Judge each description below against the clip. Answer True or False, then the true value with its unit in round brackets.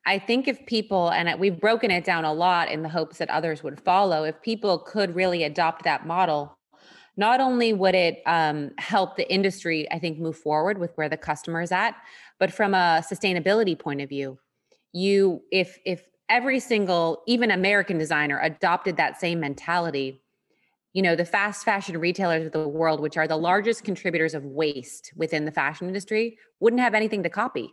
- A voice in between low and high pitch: True (175 Hz)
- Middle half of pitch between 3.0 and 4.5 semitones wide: True (3.8 semitones)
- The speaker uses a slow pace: False (190 wpm)